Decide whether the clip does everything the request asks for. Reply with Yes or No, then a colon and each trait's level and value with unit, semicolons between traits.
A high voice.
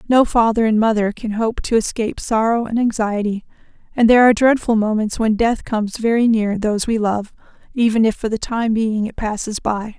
Yes: high, 220 Hz